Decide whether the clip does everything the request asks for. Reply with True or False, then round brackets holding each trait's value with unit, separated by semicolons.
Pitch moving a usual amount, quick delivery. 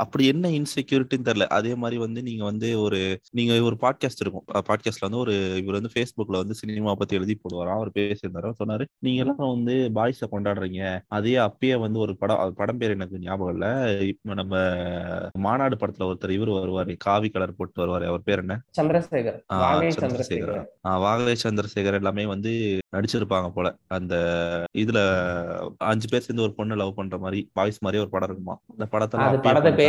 True (3.7 semitones; 165 wpm)